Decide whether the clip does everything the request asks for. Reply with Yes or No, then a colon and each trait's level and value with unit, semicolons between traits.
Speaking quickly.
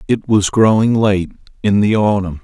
No: average, 175 wpm